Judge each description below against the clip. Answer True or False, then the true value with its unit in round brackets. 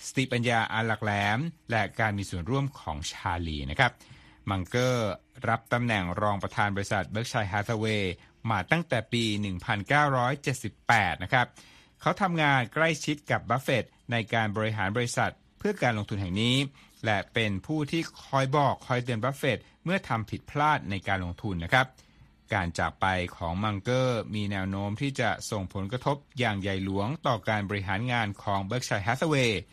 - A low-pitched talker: True (110 Hz)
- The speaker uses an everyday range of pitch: True (4.6 semitones)